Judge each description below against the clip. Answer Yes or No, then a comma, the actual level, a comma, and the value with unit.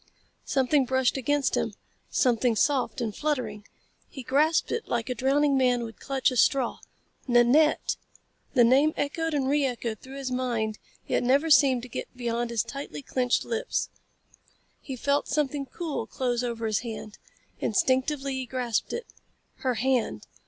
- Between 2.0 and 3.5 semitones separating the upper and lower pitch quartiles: Yes, average, 2.8 semitones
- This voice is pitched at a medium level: No, very high, 260 Hz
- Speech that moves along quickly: No, average, 155 wpm